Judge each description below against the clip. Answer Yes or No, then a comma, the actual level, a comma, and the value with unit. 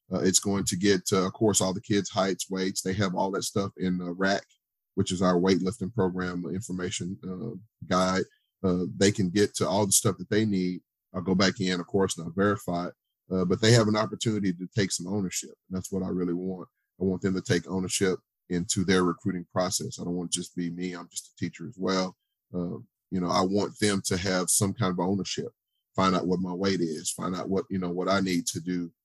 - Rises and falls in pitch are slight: Yes, narrow, 1.5 semitones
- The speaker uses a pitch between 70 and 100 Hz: Yes, very low, 95 Hz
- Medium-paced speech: No, fast, 245 wpm